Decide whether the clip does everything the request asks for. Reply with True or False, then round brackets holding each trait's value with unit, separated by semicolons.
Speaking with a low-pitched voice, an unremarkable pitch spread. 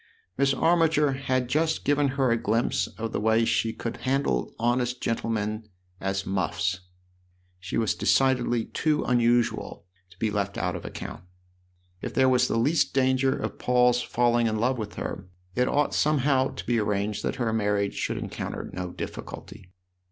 True (120 Hz; 3.6 semitones)